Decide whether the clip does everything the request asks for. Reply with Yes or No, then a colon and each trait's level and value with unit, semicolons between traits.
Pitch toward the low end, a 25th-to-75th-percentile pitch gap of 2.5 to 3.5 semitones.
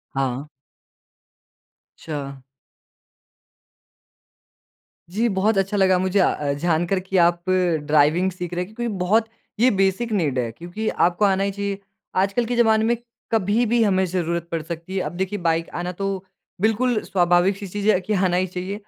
No: medium, 185 Hz; average, 3.0 semitones